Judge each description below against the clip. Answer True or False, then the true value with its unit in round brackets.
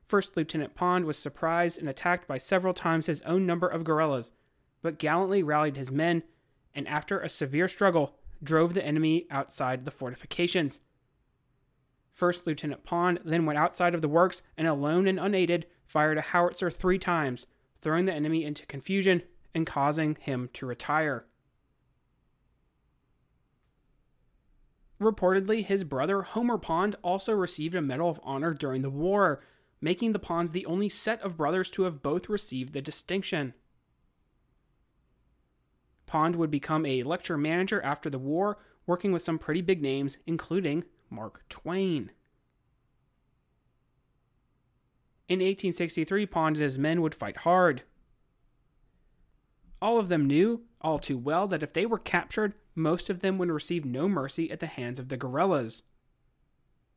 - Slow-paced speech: False (145 wpm)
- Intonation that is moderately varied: True (4.2 semitones)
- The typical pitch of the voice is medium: True (165 Hz)